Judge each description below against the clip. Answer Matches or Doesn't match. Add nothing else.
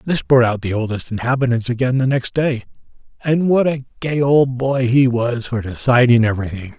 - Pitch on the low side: Matches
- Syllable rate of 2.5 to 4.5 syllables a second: Doesn't match